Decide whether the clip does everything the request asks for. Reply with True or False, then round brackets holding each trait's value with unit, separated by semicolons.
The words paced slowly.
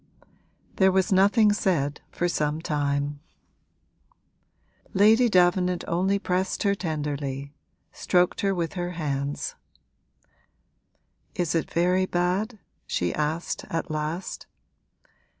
True (100 wpm)